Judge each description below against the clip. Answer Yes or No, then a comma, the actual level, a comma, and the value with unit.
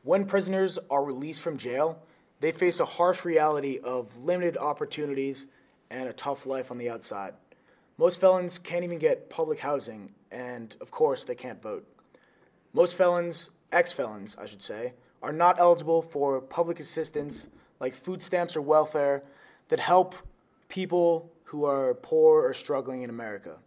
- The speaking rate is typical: Yes, average, 155 wpm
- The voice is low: No, medium, 165 Hz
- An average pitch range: Yes, average, 4.8 semitones